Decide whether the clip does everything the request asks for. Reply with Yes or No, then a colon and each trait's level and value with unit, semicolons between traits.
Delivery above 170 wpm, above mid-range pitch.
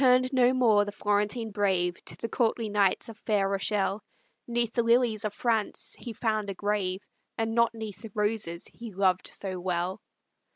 Yes: average, 180 wpm; high, 210 Hz